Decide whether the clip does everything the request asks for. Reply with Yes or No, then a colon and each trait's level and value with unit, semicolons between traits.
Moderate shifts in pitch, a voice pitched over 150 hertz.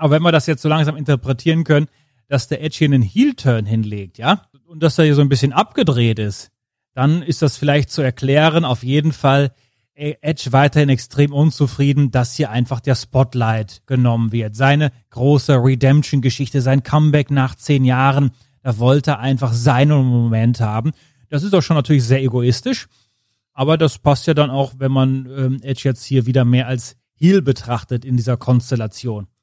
No: average, 3.2 semitones; low, 135 Hz